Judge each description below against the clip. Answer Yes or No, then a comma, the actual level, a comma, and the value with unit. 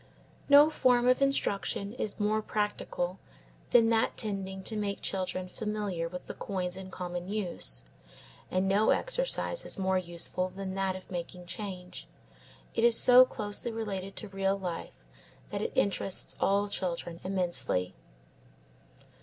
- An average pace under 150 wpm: Yes, average, 140 wpm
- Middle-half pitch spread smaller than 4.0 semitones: Yes, average, 2.9 semitones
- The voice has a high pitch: Yes, high, 195 Hz